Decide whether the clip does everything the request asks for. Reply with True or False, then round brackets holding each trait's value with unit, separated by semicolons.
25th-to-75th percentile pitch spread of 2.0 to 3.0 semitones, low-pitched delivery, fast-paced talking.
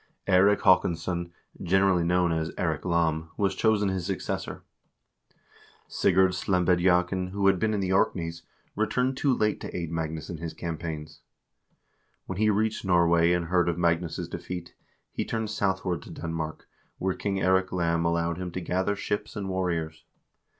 False (2.4 semitones; 90 Hz; 155 wpm)